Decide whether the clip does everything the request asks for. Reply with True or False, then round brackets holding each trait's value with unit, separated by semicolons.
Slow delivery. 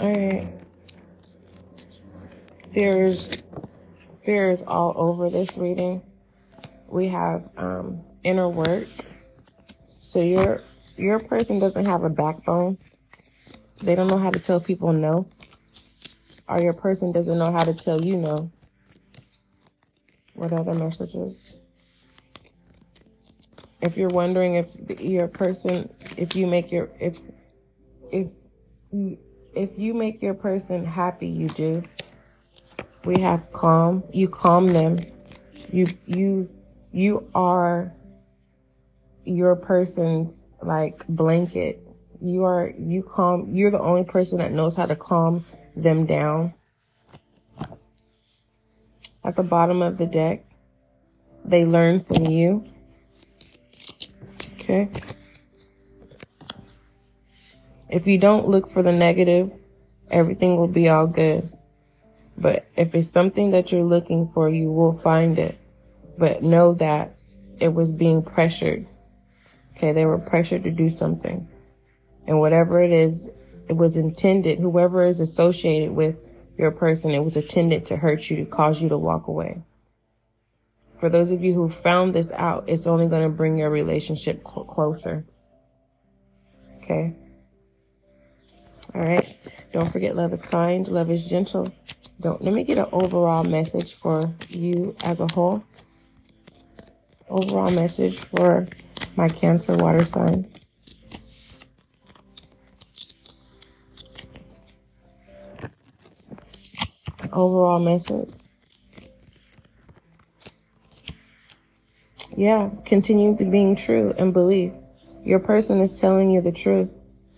True (115 wpm)